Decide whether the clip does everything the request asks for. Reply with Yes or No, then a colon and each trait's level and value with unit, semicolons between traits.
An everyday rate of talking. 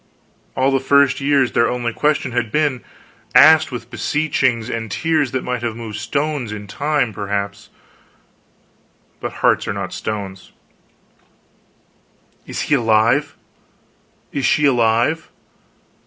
No: slow, 125 wpm